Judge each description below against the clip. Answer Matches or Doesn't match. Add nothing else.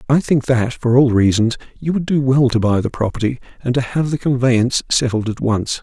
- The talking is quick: Matches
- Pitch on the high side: Doesn't match